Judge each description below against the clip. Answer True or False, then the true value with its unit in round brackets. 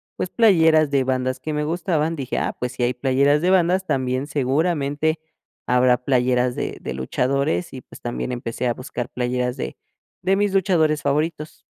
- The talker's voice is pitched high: False (140 Hz)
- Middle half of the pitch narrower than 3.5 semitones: False (4.2 semitones)